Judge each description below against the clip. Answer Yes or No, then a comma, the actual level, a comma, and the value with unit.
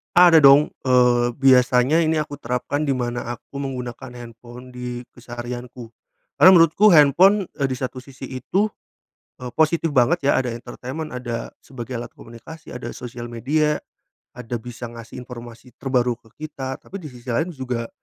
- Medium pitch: No, low, 125 Hz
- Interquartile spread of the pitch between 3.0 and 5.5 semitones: Yes, average, 3.4 semitones